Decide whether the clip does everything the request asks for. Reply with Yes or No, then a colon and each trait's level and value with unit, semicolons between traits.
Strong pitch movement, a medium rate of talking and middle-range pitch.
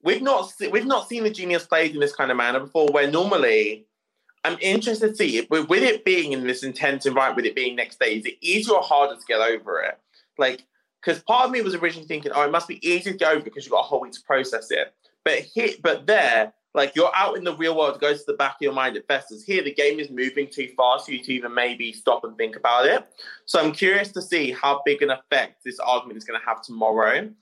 No: wide, 8.1 semitones; fast, 265 wpm; medium, 150 Hz